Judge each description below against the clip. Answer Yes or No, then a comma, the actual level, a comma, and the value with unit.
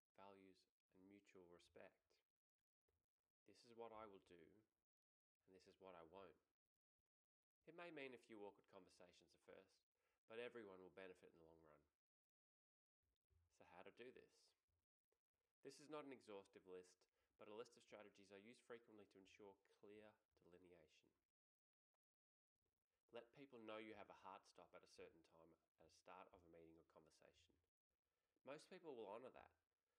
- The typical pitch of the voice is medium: No, very low, 95 Hz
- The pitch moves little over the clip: No, average, 3.6 semitones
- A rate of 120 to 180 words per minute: Yes, average, 160 wpm